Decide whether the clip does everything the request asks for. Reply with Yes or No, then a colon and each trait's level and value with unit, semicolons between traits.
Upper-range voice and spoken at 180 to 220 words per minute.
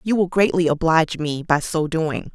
No: medium, 165 Hz; fast, 205 wpm